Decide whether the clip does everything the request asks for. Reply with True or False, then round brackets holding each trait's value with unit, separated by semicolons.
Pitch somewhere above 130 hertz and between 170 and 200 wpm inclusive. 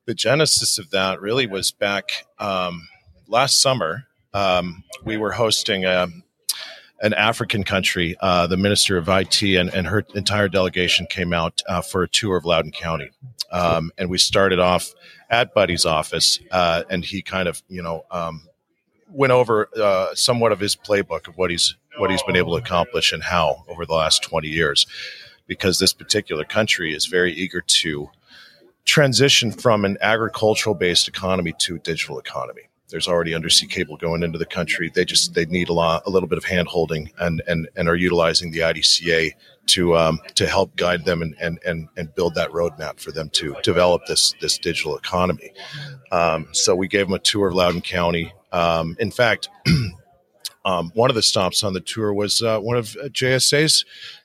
False (90 Hz; 185 wpm)